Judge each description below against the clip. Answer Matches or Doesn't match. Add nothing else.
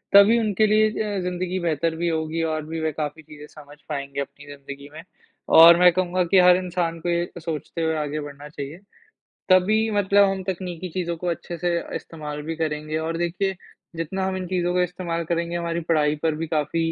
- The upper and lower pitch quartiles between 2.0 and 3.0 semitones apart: Matches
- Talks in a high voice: Doesn't match